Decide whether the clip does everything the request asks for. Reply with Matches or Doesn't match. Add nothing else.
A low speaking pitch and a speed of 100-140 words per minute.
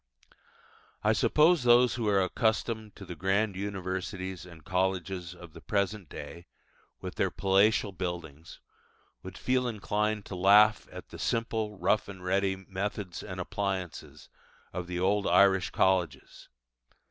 Matches